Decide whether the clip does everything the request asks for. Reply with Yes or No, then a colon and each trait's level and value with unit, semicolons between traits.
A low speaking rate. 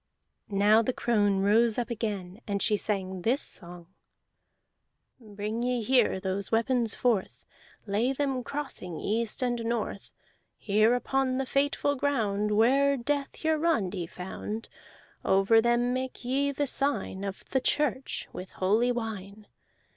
Yes: slow, 130 wpm